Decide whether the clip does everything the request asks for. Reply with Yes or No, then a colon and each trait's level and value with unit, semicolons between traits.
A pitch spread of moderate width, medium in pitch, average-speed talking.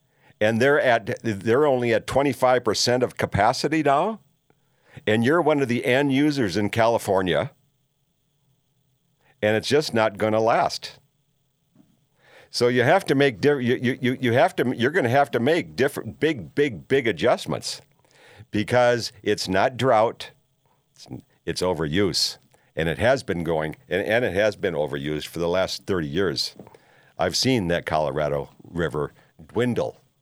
No: average, 4.2 semitones; low, 130 Hz; average, 155 wpm